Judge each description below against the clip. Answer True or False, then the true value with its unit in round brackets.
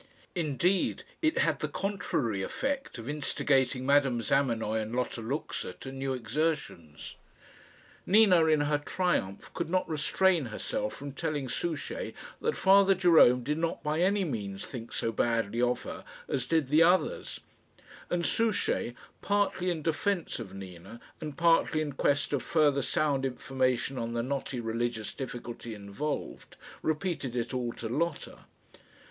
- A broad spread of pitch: True (5.9 semitones)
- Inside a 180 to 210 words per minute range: False (145 wpm)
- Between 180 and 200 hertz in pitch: False (140 Hz)